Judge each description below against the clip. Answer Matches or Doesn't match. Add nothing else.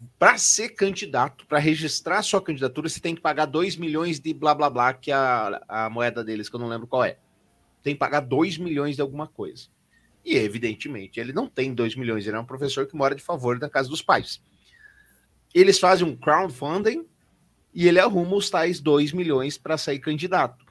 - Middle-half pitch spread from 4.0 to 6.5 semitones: Matches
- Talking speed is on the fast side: Matches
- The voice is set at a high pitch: Doesn't match